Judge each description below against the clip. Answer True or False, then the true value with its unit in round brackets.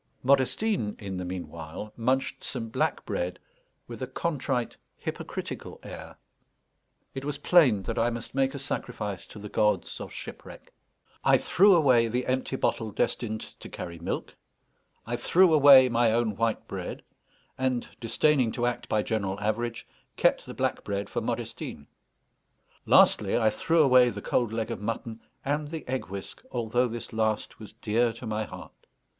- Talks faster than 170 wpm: False (160 wpm)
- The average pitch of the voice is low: True (115 Hz)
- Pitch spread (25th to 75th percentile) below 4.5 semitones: True (3.6 semitones)